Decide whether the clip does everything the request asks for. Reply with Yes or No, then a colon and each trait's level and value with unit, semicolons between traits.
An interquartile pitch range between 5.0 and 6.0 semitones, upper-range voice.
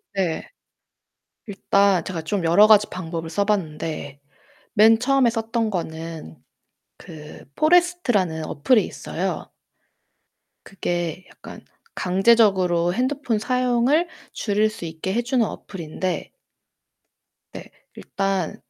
Yes: wide, 5.4 semitones; high, 195 Hz